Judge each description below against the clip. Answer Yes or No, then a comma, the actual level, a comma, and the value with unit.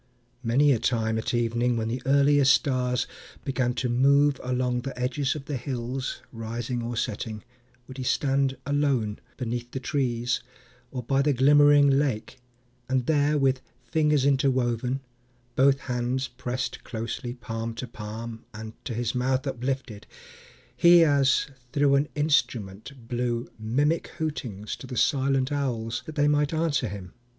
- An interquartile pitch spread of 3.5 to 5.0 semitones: No, average, 2.8 semitones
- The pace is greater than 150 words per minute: No, average, 145 wpm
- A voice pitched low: Yes, low, 130 Hz